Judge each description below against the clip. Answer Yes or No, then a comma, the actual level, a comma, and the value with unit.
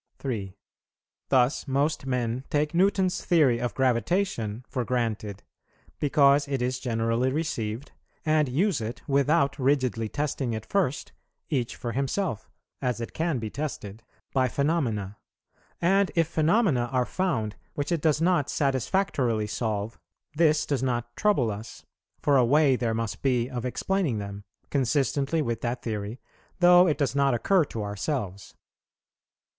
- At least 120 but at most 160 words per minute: Yes, average, 140 wpm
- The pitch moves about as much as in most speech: Yes, average, 4.7 semitones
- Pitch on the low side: Yes, low, 130 Hz